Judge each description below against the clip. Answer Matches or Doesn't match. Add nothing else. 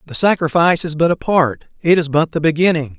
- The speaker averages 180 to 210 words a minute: Matches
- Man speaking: Matches